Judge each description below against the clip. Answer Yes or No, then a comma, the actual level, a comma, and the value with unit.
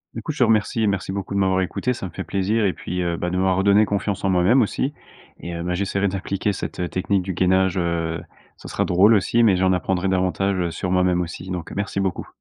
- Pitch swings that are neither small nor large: No, narrow, 1.7 semitones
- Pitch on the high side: No, very low, 95 Hz